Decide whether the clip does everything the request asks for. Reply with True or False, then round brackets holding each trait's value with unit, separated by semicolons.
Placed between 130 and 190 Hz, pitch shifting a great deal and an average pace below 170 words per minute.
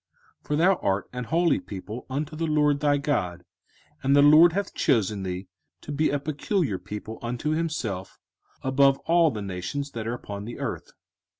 False (140 Hz; 6.7 semitones; 180 wpm)